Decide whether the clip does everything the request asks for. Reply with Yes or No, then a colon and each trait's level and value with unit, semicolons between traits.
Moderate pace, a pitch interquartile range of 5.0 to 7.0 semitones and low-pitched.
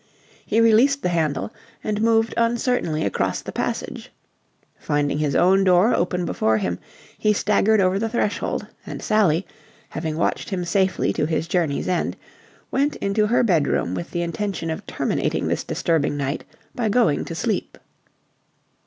No: average, 155 wpm; wide, 5.5 semitones; medium, 185 Hz